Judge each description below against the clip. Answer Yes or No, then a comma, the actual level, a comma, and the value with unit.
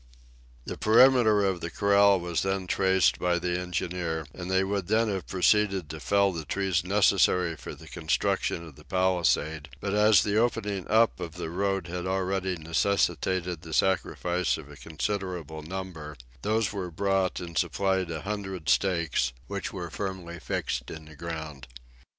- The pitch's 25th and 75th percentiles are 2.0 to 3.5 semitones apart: Yes, average, 2.9 semitones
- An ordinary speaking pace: Yes, average, 160 wpm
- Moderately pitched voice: No, very low, 90 Hz